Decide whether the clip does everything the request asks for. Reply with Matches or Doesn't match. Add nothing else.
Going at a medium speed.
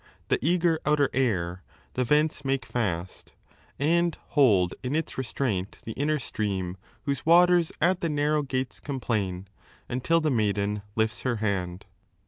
Matches